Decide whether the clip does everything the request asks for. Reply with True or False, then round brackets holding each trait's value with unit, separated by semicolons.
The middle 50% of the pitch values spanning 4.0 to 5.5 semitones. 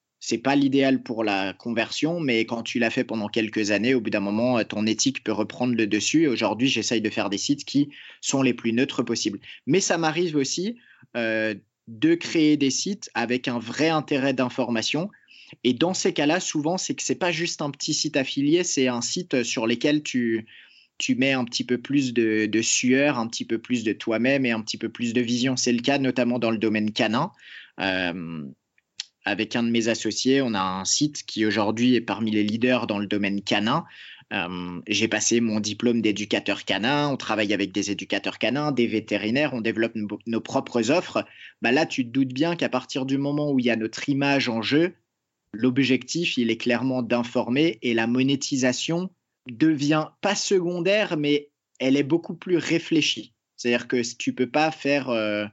True (4.3 semitones)